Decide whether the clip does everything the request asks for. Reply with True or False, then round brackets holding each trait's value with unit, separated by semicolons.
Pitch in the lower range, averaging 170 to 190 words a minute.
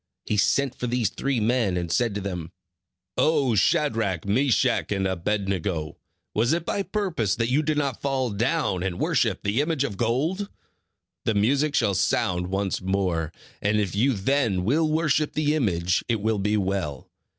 True (110 Hz; 175 wpm)